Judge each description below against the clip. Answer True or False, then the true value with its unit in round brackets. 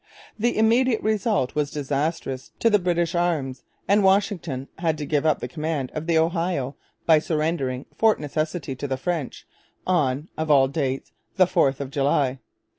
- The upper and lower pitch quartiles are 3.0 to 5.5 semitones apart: True (4.3 semitones)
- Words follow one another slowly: False (165 wpm)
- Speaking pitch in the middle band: True (155 Hz)